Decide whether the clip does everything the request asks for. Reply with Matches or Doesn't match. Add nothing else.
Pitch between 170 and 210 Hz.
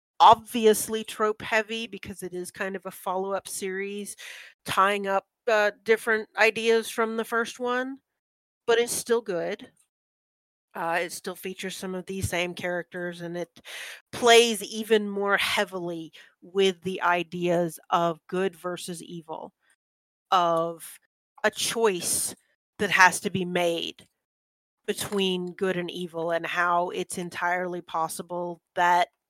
Matches